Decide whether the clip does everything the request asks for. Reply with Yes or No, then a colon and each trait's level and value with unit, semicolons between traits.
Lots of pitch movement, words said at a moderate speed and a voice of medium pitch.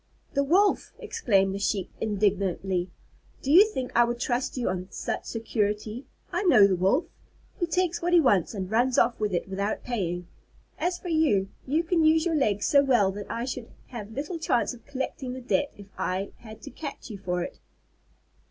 No: wide, 6.3 semitones; average, 195 wpm; high, 235 Hz